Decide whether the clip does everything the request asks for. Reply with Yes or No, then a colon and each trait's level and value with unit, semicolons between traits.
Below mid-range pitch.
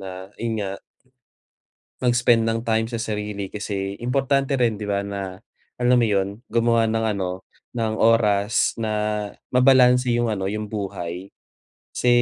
Yes: low, 110 Hz